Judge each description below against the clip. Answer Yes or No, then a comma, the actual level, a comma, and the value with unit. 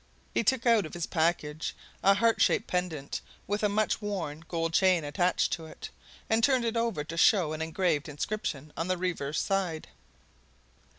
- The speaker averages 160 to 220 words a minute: Yes, average, 175 wpm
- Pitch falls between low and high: Yes, medium, 180 Hz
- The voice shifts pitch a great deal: No, average, 4.6 semitones